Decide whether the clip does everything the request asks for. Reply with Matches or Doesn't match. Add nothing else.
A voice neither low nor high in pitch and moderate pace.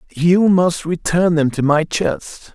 Matches